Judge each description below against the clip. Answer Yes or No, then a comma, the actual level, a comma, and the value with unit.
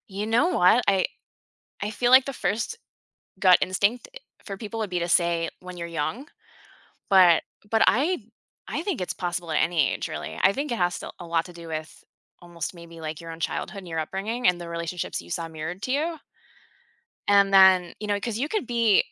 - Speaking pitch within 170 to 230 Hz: Yes, medium, 185 Hz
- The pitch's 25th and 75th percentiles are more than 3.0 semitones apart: Yes, average, 4.9 semitones